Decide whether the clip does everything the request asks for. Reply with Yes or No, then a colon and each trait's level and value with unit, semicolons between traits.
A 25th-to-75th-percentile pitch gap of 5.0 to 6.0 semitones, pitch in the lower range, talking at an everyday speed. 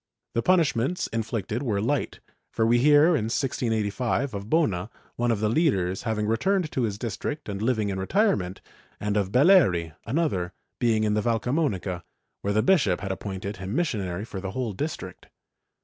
Yes: wide, 5.4 semitones; low, 110 Hz; average, 170 wpm